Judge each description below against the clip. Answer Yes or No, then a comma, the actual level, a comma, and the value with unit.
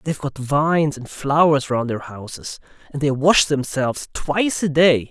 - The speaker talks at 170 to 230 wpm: Yes, average, 175 wpm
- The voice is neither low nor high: Yes, medium, 145 Hz